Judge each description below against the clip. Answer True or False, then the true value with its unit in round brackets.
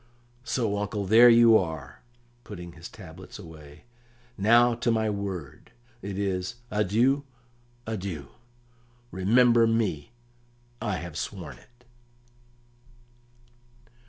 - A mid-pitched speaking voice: False (100 Hz)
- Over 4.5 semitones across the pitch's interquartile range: False (4.2 semitones)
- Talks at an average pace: False (100 wpm)